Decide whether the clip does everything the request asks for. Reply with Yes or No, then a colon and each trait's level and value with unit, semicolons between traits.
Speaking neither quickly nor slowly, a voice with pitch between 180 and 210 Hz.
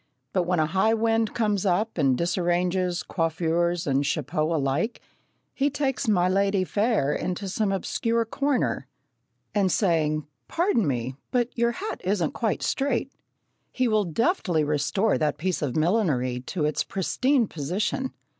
Yes: average, 145 wpm; medium, 185 Hz